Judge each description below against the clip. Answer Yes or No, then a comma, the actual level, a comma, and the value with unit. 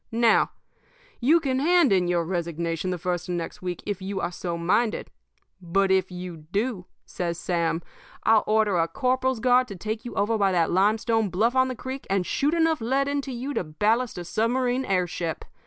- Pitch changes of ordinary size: No, wide, 6.1 semitones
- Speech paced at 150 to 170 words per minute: No, average, 195 wpm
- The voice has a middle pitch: No, high, 205 Hz